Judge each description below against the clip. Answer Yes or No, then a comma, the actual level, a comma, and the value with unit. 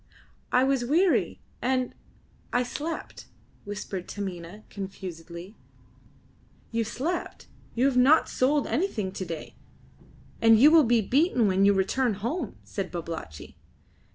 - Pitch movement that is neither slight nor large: No, wide, 5.7 semitones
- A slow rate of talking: Yes, slow, 125 wpm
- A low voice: No, high, 230 Hz